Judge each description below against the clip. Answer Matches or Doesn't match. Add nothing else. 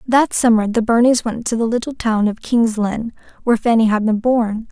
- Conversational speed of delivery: Doesn't match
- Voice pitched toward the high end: Matches